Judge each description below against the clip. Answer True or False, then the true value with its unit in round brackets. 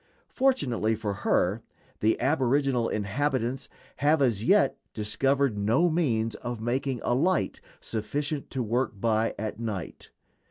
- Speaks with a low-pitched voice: True (120 Hz)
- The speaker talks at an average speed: False (125 wpm)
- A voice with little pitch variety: False (4.2 semitones)